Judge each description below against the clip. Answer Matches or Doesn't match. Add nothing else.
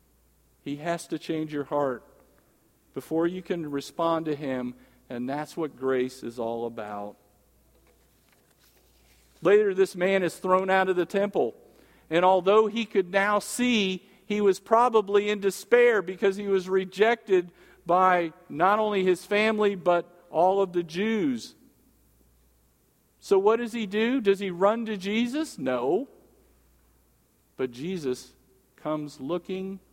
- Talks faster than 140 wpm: Doesn't match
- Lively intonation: Matches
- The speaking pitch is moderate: Matches